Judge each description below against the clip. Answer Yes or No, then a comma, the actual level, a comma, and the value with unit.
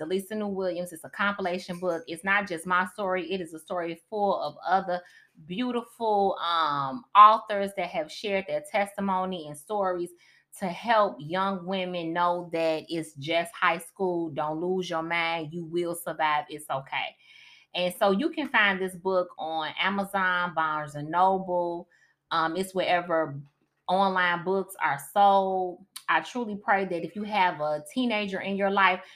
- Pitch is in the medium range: Yes, medium, 180 Hz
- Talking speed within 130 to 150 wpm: No, average, 165 wpm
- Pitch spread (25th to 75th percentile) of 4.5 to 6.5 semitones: No, average, 2.7 semitones